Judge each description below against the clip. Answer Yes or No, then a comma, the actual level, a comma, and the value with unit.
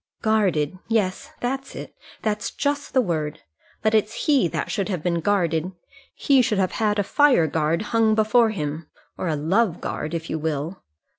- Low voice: No, high, 195 Hz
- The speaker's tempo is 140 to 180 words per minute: Yes, average, 175 wpm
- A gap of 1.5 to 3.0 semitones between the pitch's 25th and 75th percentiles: No, wide, 5.6 semitones